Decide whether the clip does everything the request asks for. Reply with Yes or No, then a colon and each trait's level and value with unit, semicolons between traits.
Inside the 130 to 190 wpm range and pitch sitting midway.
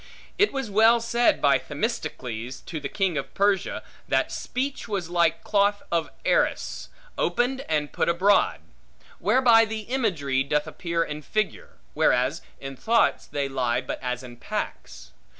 Yes: average, 150 wpm; medium, 175 Hz